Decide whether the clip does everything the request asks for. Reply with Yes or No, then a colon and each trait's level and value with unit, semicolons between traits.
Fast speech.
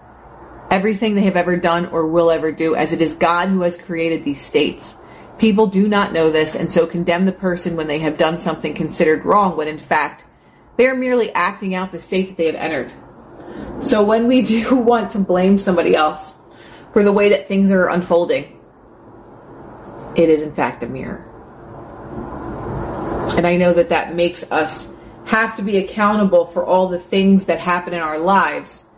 No: average, 190 wpm